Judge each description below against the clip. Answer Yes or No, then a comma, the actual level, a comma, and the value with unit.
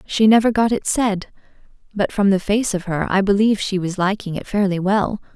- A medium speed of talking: No, fast, 215 wpm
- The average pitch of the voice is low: No, high, 200 Hz